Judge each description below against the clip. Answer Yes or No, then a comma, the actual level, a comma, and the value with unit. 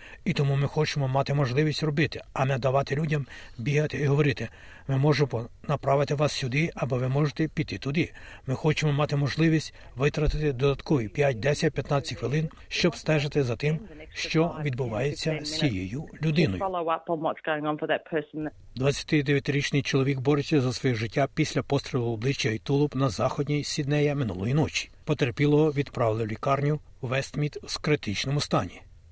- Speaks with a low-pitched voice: No, medium, 145 Hz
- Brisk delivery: No, average, 140 wpm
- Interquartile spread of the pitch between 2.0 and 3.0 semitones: Yes, narrow, 2.4 semitones